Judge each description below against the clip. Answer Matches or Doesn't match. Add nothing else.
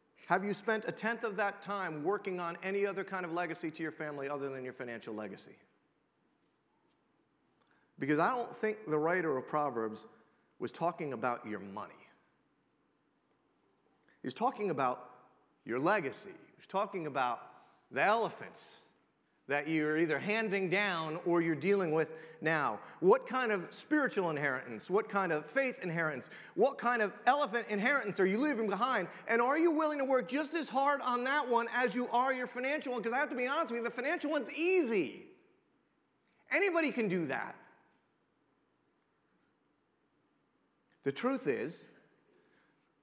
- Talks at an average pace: Matches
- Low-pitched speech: Doesn't match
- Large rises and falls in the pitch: Matches